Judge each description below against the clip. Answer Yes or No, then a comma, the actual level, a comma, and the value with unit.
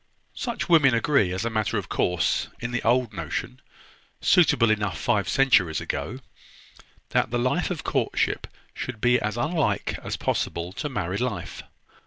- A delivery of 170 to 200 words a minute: No, average, 155 wpm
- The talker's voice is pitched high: No, low, 115 Hz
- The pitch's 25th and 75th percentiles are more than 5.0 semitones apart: Yes, wide, 5.6 semitones